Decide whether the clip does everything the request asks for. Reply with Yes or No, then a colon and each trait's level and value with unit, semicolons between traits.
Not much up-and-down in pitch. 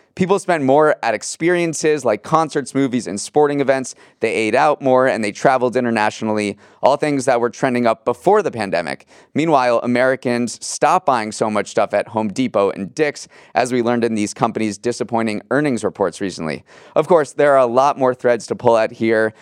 No: average, 3.9 semitones